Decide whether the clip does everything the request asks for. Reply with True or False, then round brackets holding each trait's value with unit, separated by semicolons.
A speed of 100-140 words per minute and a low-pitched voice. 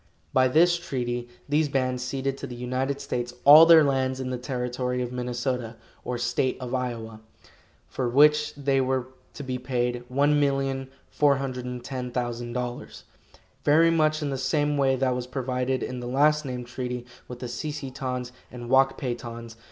False (160 wpm; 130 Hz)